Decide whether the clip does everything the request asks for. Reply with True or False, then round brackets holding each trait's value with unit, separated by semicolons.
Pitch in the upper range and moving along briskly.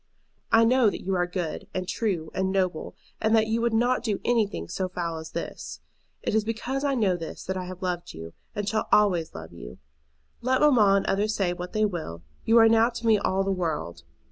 True (195 Hz; 220 wpm)